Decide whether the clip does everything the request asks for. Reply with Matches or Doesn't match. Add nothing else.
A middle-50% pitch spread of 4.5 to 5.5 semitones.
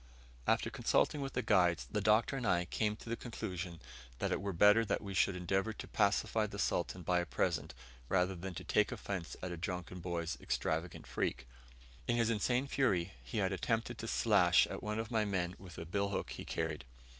Doesn't match